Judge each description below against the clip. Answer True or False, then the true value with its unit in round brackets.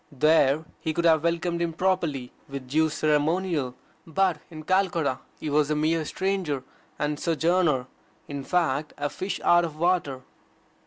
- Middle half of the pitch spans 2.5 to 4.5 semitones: True (3.0 semitones)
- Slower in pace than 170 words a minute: True (150 wpm)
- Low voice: False (155 Hz)